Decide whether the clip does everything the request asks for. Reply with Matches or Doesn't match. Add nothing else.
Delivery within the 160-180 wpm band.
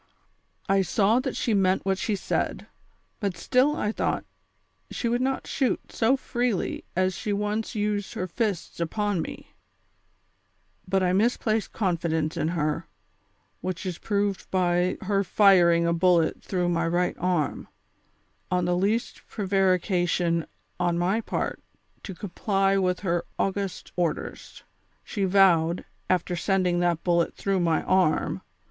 Doesn't match